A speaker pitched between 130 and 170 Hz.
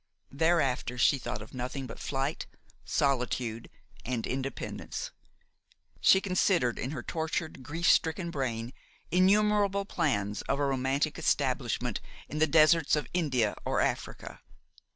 Yes: medium, 140 Hz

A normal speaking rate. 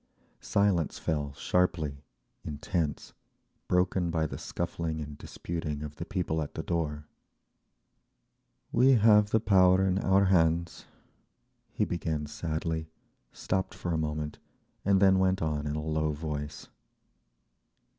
No: slow, 125 wpm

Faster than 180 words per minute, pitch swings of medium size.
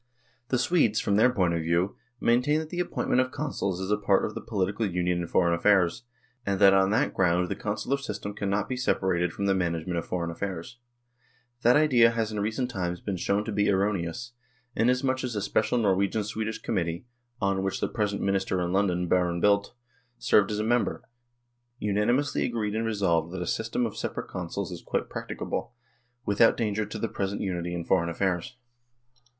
Yes: average, 190 wpm; average, 3.8 semitones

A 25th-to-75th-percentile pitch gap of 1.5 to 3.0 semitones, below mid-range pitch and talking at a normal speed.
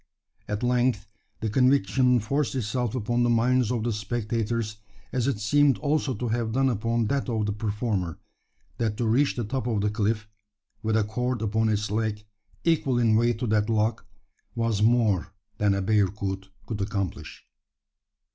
Yes: average, 2.7 semitones; low, 115 Hz; average, 165 wpm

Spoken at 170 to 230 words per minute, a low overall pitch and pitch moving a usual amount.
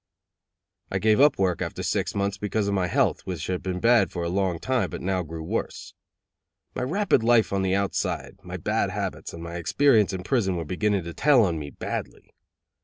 Yes: fast, 205 wpm; very low, 95 Hz; average, 3.6 semitones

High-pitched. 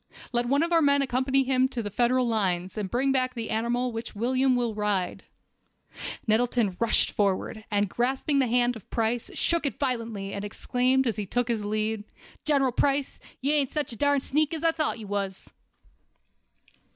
Yes: high, 245 Hz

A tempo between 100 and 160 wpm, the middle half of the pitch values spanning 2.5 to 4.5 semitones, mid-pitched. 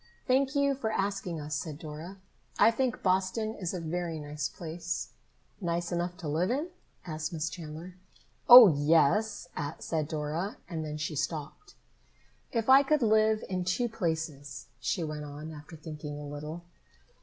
No: average, 155 wpm; wide, 5.6 semitones; medium, 170 Hz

